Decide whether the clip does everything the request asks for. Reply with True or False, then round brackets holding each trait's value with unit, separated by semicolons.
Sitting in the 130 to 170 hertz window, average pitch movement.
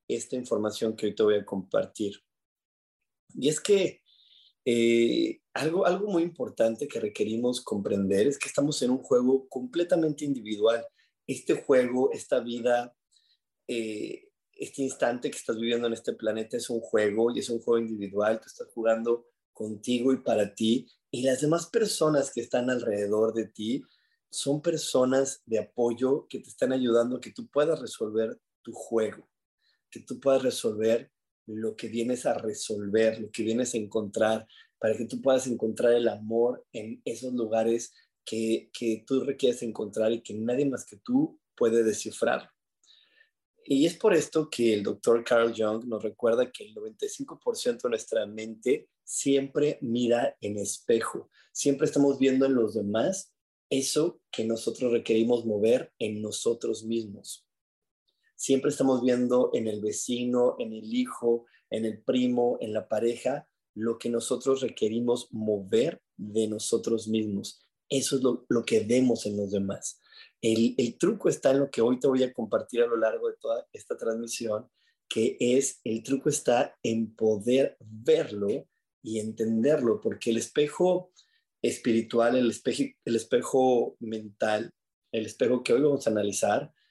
False (120 Hz; 4.0 semitones)